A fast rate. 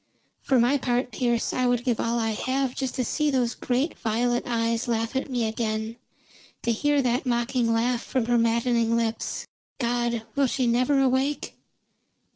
No: average, 170 wpm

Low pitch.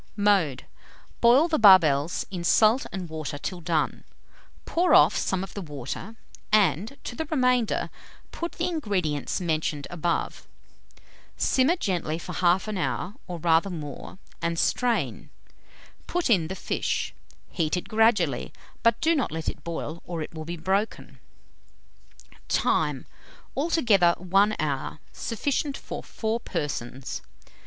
No: medium, 185 Hz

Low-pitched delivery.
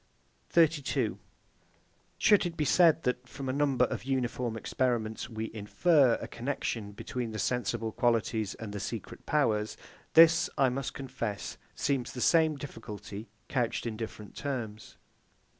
Yes: low, 125 Hz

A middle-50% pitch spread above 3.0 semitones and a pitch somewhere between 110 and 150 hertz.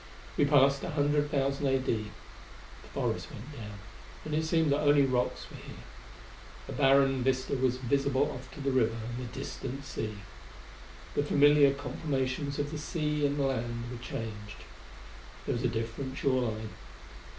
No: average, 2.7 semitones; low, 135 Hz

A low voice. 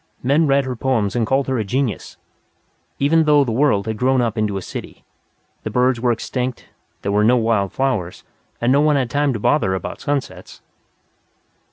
Yes: low, 125 Hz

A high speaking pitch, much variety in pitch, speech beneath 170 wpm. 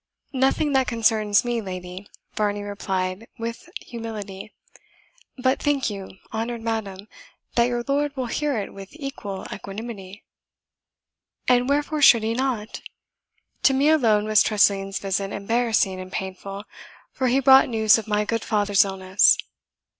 No: high, 220 Hz; average, 4.0 semitones; average, 140 wpm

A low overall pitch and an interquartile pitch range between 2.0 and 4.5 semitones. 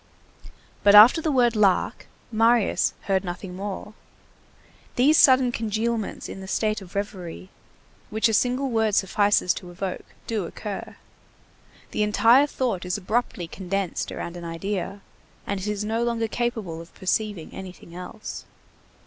No: high, 205 Hz; average, 3.4 semitones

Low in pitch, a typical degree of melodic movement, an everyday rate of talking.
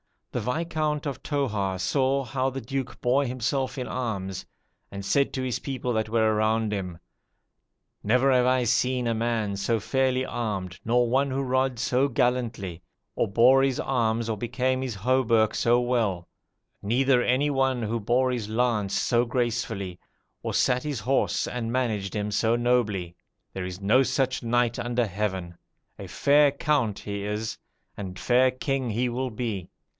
Yes: low, 120 Hz; average, 3.4 semitones; average, 165 wpm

